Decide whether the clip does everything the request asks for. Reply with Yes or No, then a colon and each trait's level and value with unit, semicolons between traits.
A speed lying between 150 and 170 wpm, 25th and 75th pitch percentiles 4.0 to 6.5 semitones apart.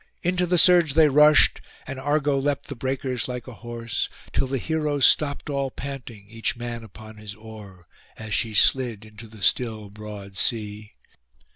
Yes: average, 165 wpm; average, 4.6 semitones